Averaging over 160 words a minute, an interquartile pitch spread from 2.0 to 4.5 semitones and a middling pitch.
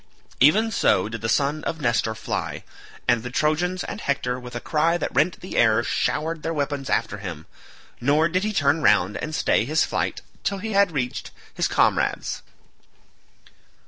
No: average, 175 wpm; wide, 5.5 semitones; medium, 145 Hz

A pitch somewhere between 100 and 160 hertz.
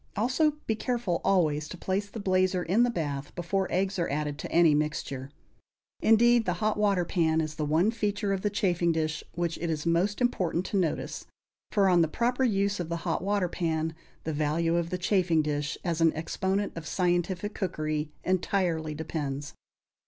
No: medium, 175 Hz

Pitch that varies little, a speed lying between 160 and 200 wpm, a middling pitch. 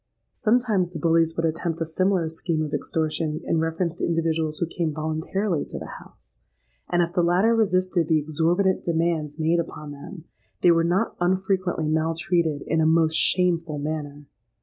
Yes: narrow, 2.0 semitones; average, 170 wpm; medium, 165 Hz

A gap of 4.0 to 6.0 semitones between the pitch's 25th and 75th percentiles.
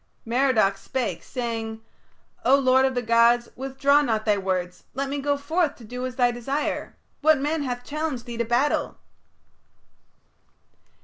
No: average, 3.1 semitones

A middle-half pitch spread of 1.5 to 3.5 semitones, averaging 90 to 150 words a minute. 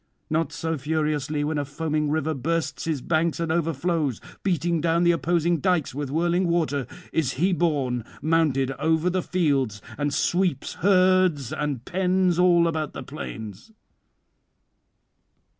Yes: average, 3.0 semitones; average, 140 wpm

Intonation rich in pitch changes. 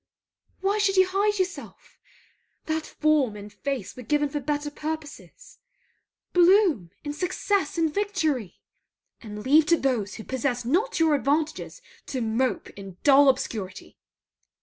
Yes: wide, 6.0 semitones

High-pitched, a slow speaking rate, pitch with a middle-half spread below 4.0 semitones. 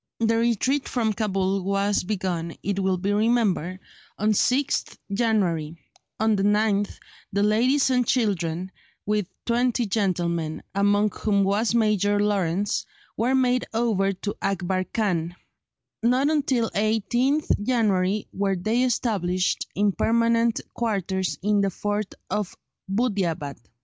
Yes: high, 205 Hz; slow, 125 wpm; average, 3.3 semitones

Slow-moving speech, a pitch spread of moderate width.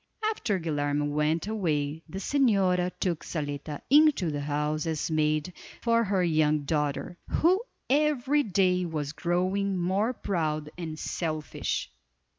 Yes: slow, 125 wpm; average, 4.7 semitones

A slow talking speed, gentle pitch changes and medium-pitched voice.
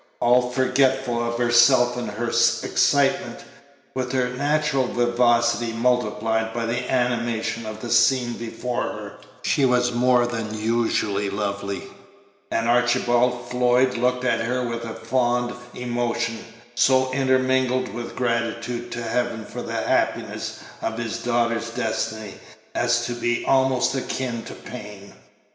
No: slow, 130 wpm; narrow, 1.3 semitones; low, 120 Hz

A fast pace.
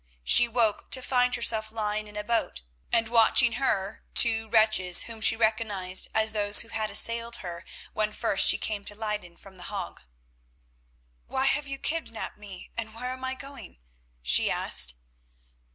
No: average, 170 wpm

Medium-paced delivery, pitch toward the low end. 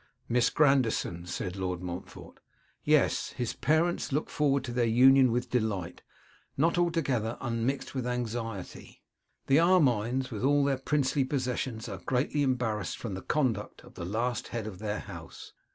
Yes: average, 150 wpm; low, 125 Hz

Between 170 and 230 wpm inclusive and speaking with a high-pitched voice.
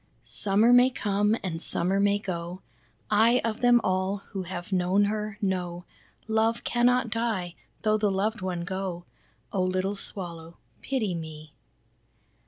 No: average, 140 wpm; high, 195 Hz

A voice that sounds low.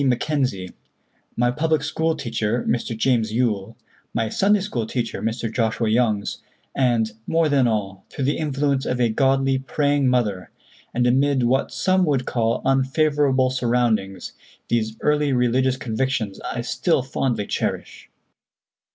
Yes: low, 125 Hz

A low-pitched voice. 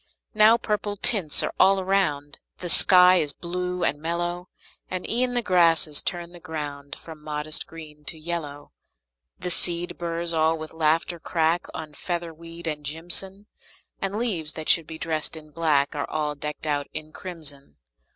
No: medium, 165 Hz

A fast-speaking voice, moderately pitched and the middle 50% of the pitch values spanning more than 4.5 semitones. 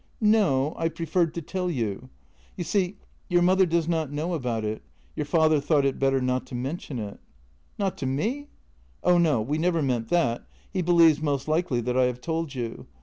Yes: fast, 210 wpm; medium, 150 Hz; average, 5.2 semitones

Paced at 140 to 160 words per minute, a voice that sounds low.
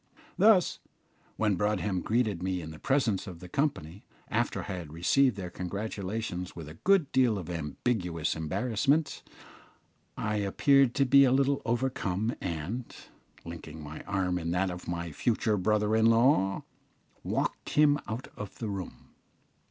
Yes: average, 150 wpm; low, 105 Hz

